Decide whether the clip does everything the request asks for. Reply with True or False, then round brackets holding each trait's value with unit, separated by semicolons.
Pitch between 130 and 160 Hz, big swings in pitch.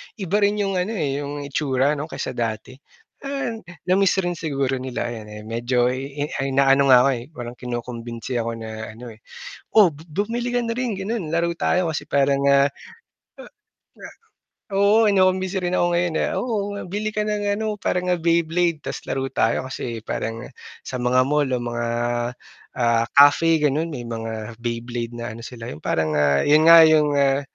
True (140 Hz; 7.1 semitones)